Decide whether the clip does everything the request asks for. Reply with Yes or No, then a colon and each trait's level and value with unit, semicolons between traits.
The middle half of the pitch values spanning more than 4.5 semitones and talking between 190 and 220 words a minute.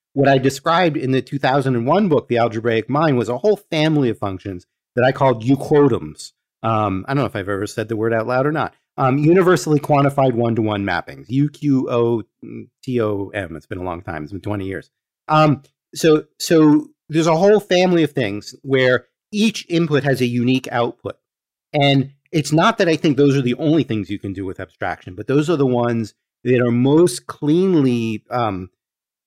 Yes: average, 5.1 semitones; average, 195 wpm